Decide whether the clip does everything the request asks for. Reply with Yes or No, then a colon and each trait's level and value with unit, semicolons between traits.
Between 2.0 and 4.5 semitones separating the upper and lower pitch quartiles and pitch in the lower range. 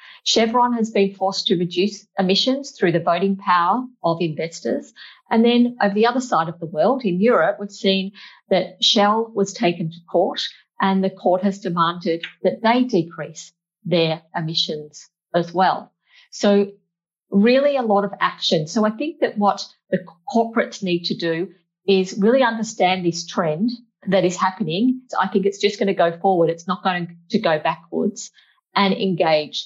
No: average, 3.8 semitones; high, 195 Hz